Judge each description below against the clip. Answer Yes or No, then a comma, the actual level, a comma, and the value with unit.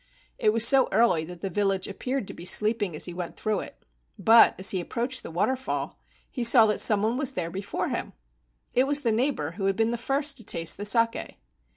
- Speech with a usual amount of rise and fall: Yes, average, 4.5 semitones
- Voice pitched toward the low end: No, high, 220 Hz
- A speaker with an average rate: No, fast, 230 wpm